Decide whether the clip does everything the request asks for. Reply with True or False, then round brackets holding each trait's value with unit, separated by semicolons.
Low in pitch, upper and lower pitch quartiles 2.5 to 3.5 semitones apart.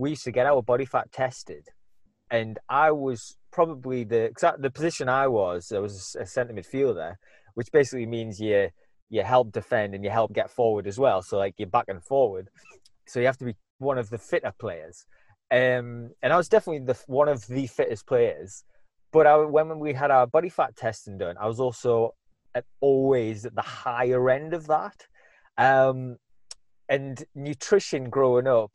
False (125 Hz; 4.3 semitones)